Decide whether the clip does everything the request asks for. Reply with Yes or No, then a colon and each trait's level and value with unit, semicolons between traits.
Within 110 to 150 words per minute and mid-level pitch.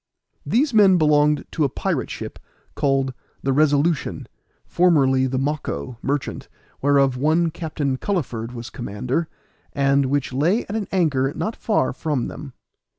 Yes: average, 140 wpm; medium, 145 Hz